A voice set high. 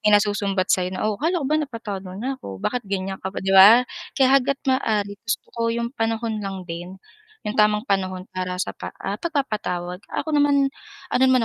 Yes: high, 210 Hz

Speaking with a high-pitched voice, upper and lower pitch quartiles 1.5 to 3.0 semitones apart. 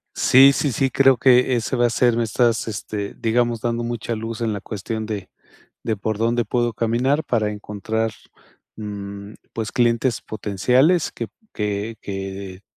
No: low, 115 Hz; narrow, 2.5 semitones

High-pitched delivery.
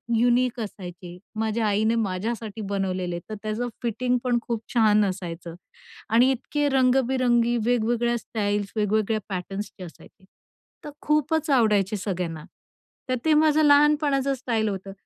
Yes: high, 225 Hz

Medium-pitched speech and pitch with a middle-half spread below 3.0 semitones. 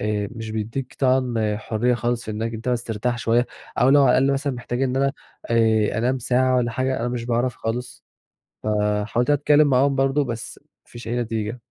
No: low, 120 Hz; narrow, 2.5 semitones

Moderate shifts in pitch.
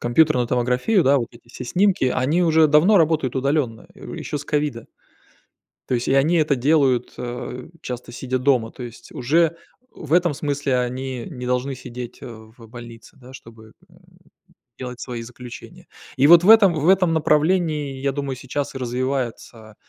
Yes: average, 3.8 semitones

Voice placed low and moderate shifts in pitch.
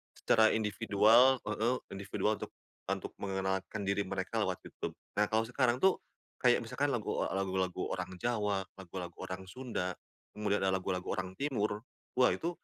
Yes: low, 105 Hz; average, 3.0 semitones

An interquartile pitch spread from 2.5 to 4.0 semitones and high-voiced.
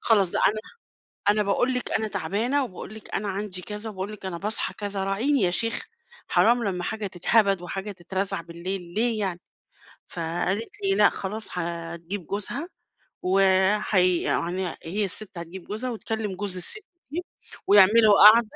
Yes: average, 3.2 semitones; high, 200 Hz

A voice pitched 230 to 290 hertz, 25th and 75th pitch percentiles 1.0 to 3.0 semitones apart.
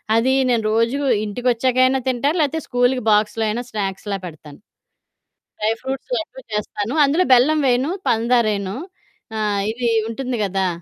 No: high, 235 Hz; average, 3.6 semitones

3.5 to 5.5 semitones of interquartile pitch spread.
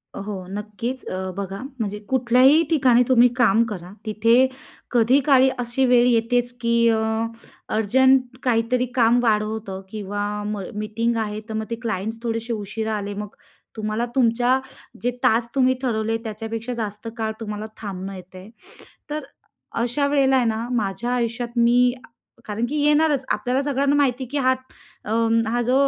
No: average, 2.8 semitones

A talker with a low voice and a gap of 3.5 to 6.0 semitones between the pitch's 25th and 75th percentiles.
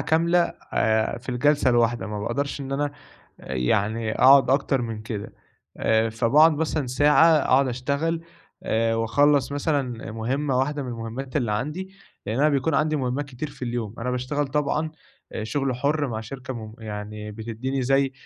Yes: low, 130 Hz; average, 4.2 semitones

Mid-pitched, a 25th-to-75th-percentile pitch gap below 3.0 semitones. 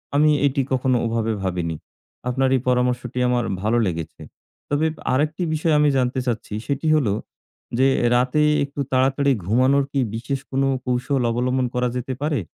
No: low, 130 Hz; narrow, 2.4 semitones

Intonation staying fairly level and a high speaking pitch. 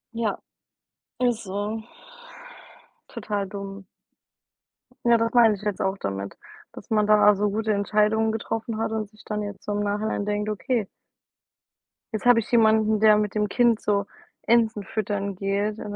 Yes: narrow, 1.4 semitones; high, 210 Hz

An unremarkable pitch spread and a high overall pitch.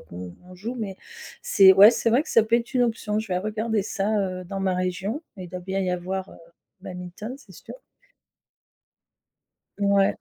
Yes: average, 3.3 semitones; high, 195 Hz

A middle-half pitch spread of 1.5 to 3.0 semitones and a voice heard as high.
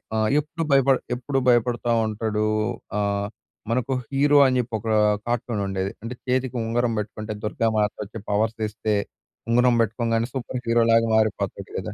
No: narrow, 2.6 semitones; low, 115 Hz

